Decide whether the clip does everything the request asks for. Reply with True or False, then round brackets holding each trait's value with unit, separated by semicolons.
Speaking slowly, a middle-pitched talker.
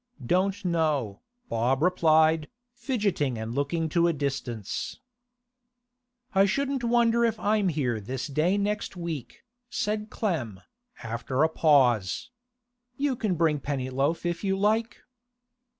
True (120 wpm; 160 Hz)